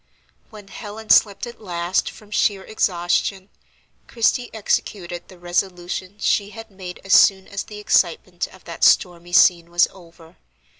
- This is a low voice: No, high, 190 Hz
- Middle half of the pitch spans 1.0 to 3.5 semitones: Yes, average, 2.9 semitones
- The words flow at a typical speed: Yes, average, 145 wpm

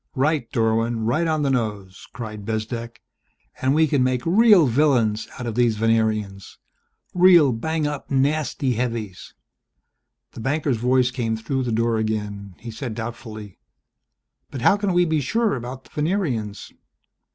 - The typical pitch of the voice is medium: No, low, 120 Hz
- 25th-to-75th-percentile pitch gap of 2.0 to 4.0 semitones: No, average, 4.8 semitones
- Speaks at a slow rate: No, average, 150 wpm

